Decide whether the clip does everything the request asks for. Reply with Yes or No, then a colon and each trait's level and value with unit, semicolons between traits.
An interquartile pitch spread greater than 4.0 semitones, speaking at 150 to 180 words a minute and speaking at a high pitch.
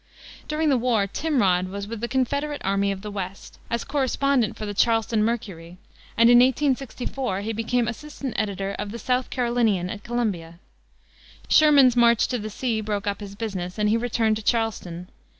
No: average, 3.7 semitones; average, 175 wpm; high, 225 Hz